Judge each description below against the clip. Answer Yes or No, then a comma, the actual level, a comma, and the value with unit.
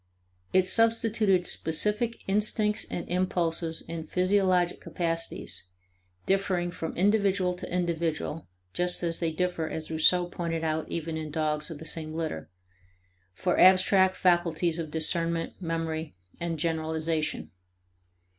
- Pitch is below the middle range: No, medium, 170 Hz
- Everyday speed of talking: No, slow, 120 wpm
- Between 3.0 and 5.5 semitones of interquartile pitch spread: No, narrow, 2.4 semitones